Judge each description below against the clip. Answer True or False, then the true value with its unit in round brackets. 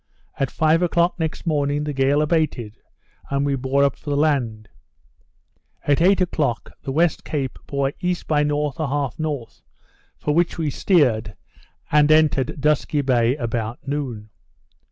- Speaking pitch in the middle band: True (145 Hz)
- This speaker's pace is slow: False (150 wpm)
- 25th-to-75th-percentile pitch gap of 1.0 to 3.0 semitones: True (2.7 semitones)